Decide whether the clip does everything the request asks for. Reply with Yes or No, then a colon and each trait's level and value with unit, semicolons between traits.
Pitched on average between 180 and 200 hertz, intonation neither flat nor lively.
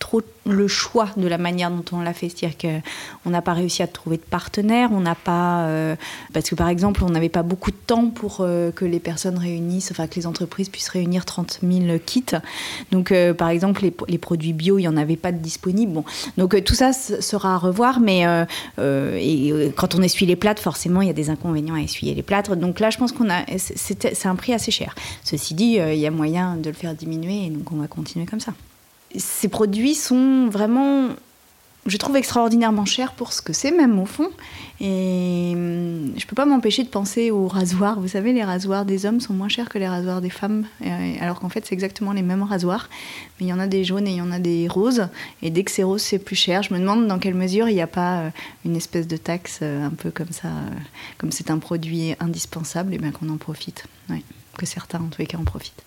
Yes: medium, 185 Hz; average, 3.6 semitones